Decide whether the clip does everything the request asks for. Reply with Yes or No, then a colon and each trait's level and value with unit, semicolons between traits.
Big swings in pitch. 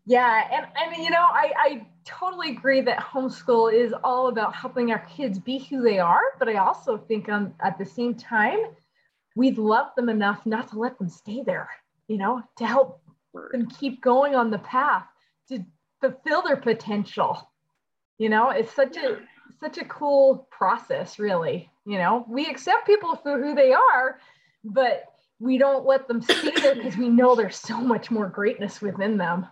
No: average, 4.2 semitones